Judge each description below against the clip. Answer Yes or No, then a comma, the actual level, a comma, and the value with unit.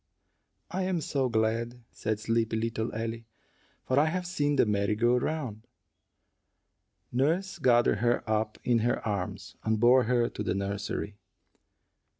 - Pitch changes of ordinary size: Yes, average, 3.1 semitones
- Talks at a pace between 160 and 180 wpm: No, average, 145 wpm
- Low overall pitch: Yes, low, 115 Hz